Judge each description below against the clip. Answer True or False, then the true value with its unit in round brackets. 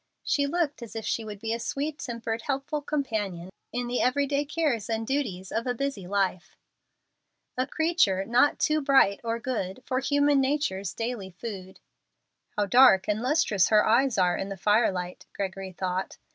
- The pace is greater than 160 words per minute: True (175 wpm)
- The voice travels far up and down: True (6.0 semitones)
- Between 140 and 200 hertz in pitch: False (230 Hz)